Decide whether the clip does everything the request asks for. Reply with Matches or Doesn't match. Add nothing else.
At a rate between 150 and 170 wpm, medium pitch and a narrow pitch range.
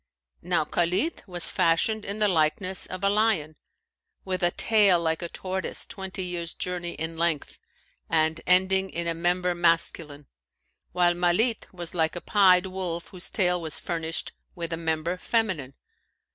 Matches